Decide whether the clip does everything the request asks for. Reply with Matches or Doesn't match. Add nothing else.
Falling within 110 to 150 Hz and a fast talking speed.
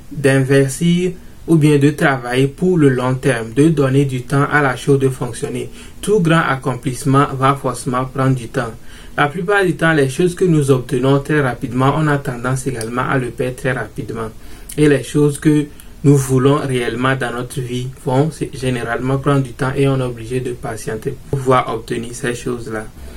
Doesn't match